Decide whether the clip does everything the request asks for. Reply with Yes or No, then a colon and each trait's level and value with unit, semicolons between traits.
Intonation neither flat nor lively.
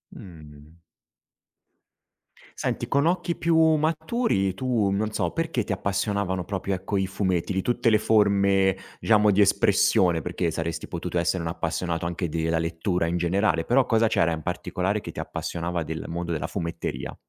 Yes: average, 3.9 semitones